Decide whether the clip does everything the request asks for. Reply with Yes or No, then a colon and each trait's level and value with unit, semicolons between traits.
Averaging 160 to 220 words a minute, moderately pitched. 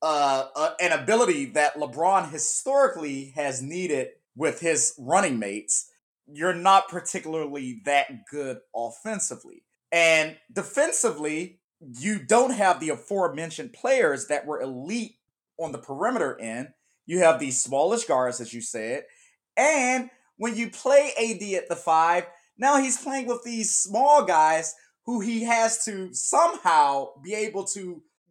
No: average, 140 wpm; medium, 180 Hz